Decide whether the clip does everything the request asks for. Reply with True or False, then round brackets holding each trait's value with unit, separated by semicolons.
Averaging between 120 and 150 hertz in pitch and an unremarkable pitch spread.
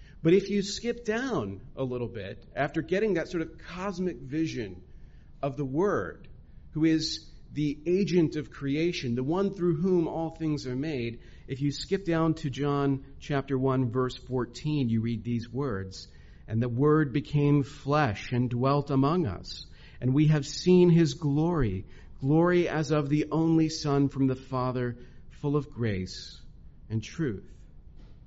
True (140 Hz; 4.7 semitones)